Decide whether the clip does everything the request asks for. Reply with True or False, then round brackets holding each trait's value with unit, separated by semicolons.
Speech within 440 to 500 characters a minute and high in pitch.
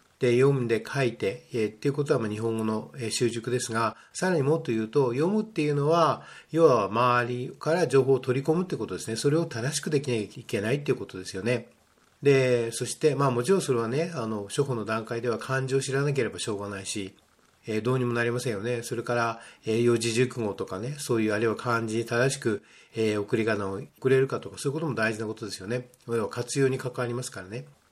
False (460 characters per minute; 120 Hz)